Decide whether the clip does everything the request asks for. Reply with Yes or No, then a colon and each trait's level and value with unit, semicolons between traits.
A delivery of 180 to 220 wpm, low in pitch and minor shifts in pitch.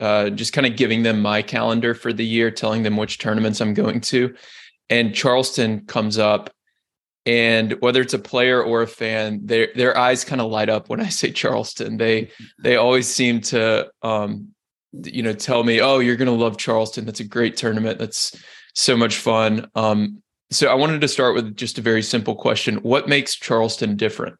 Yes: average, 200 wpm; low, 115 Hz; narrow, 2.1 semitones